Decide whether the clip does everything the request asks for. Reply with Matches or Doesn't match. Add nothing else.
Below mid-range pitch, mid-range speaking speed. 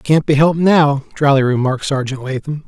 Doesn't match